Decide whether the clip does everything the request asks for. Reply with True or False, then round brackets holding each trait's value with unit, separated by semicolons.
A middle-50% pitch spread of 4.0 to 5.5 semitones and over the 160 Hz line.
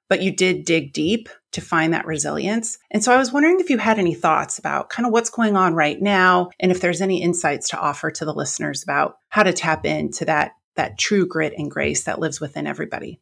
True (5.2 semitones; 185 Hz)